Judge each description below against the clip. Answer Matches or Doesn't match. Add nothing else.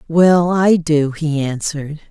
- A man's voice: Doesn't match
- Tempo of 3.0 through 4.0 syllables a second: Matches